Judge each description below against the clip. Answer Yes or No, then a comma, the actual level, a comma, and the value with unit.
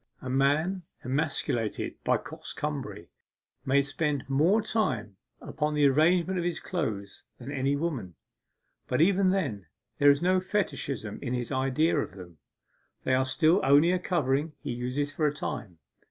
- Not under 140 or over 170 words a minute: Yes, average, 155 wpm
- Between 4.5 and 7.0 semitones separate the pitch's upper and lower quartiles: Yes, average, 4.8 semitones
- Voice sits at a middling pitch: Yes, medium, 145 Hz